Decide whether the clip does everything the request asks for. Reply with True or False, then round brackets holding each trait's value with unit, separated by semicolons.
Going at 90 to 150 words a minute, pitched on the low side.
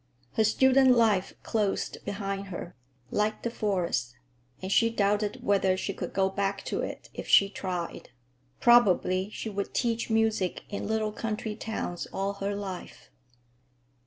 False (145 wpm; 200 Hz)